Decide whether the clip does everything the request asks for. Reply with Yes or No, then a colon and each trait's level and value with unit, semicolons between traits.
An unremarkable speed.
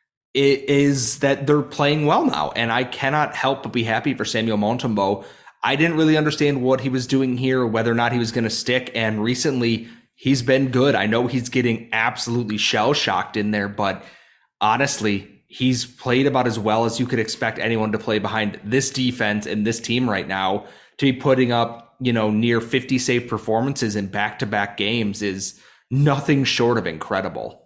Yes: average, 190 wpm